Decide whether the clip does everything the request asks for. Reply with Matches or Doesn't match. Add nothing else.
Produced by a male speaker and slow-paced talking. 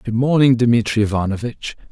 Matches